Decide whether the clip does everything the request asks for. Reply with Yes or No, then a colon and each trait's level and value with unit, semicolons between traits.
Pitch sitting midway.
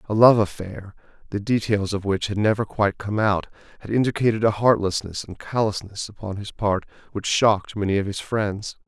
No: low, 105 Hz